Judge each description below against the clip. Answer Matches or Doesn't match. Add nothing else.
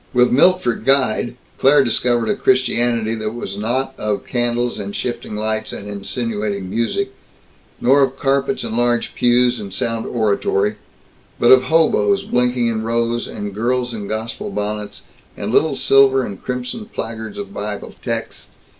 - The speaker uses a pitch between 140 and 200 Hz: Doesn't match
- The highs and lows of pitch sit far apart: Doesn't match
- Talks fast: Doesn't match